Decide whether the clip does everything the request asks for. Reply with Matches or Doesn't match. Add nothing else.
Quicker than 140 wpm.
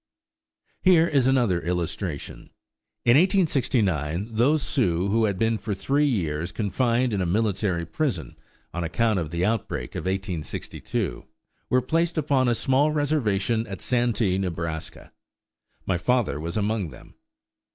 Doesn't match